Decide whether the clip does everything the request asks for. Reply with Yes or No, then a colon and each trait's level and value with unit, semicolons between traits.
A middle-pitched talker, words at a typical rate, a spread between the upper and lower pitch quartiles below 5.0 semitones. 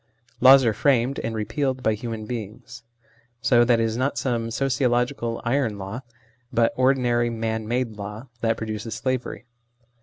No: low, 120 Hz; average, 150 wpm; narrow, 2.4 semitones